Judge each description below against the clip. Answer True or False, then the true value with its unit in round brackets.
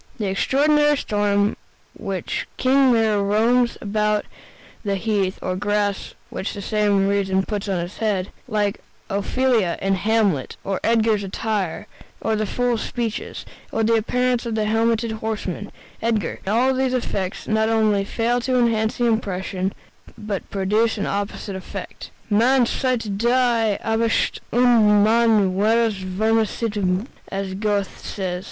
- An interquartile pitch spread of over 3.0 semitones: False (2.5 semitones)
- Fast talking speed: False (145 wpm)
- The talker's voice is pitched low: False (215 Hz)